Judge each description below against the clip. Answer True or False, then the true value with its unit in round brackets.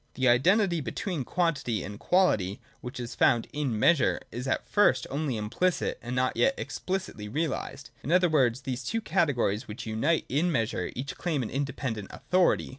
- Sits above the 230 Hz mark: False (135 Hz)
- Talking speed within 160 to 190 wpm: True (170 wpm)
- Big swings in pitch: True (6.2 semitones)